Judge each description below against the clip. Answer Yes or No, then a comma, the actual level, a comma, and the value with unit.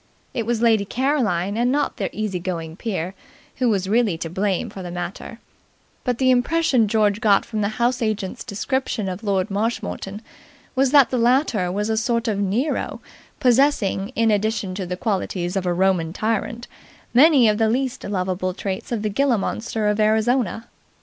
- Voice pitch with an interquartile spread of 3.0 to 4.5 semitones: Yes, average, 3.8 semitones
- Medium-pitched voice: No, high, 215 Hz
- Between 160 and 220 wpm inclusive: Yes, average, 180 wpm